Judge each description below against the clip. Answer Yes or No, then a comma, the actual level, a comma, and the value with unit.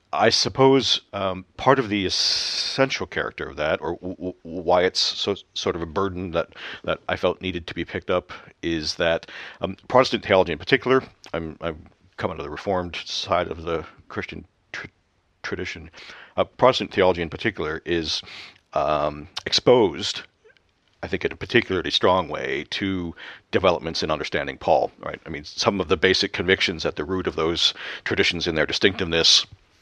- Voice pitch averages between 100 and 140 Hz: No, very low, 90 Hz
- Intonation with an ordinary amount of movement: Yes, average, 3.0 semitones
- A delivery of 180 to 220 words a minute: No, average, 170 wpm